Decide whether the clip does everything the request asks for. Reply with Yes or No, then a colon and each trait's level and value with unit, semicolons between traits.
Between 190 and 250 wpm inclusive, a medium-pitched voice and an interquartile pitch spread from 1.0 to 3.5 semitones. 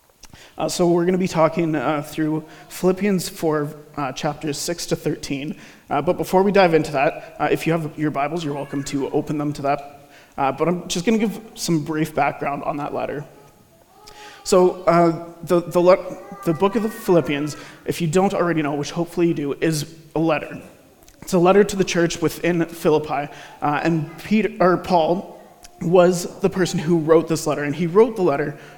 Yes: average, 200 wpm; medium, 165 Hz; average, 3.1 semitones